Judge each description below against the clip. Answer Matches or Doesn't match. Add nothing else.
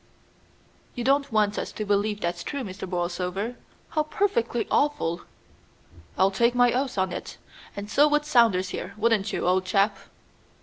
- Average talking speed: Matches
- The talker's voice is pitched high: Matches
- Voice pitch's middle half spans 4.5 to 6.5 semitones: Matches